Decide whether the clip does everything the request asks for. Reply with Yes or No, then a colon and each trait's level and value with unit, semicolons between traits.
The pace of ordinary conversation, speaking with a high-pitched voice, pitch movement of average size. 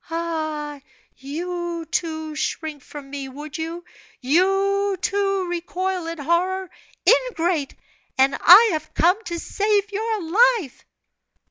No: slow, 115 wpm; very high, 340 Hz; average, 3.9 semitones